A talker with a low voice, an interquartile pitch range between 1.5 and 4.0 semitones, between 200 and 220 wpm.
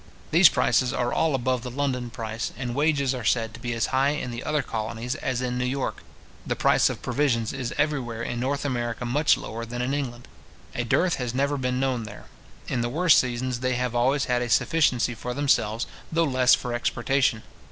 Yes: low, 125 Hz; narrow, 2.4 semitones; fast, 205 wpm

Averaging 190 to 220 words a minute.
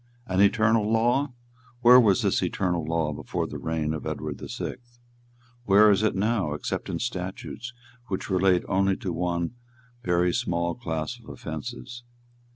No: average, 155 wpm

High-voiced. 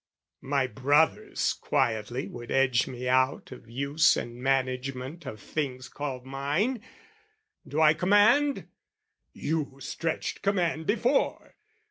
No: low, 135 Hz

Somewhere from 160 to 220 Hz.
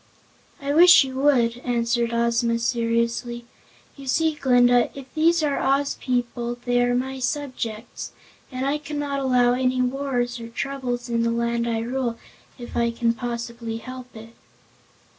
No: high, 245 Hz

